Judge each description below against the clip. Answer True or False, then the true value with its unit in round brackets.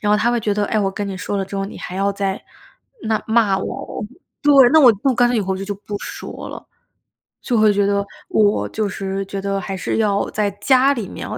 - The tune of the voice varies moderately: False (2.0 semitones)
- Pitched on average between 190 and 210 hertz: True (205 Hz)